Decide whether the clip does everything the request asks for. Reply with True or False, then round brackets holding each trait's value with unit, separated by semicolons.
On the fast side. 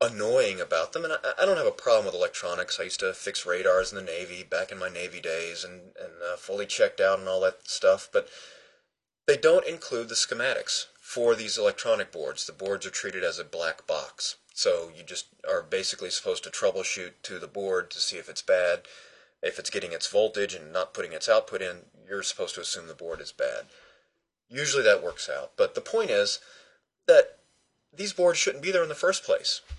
True (215 wpm)